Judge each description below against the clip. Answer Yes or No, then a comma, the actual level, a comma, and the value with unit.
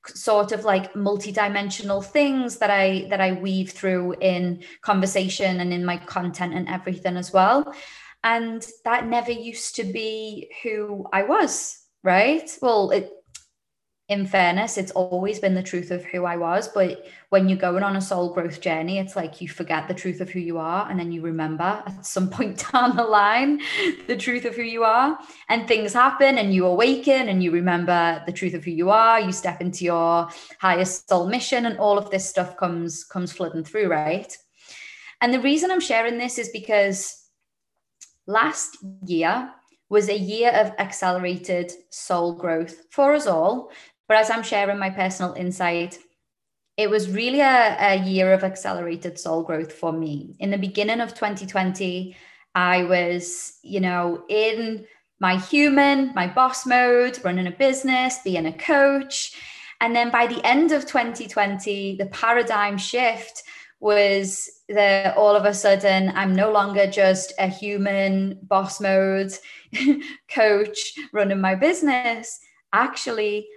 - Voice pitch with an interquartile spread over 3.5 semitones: Yes, average, 4.0 semitones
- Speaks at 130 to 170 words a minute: Yes, average, 165 wpm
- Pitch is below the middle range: No, high, 200 Hz